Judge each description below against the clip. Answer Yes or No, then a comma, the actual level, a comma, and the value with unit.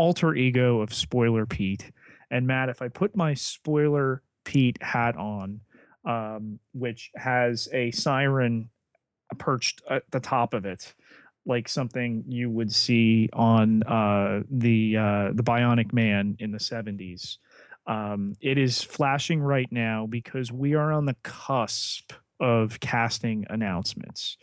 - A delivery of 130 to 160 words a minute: Yes, average, 140 wpm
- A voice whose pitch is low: Yes, low, 120 Hz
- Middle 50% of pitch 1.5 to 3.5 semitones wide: Yes, average, 2.9 semitones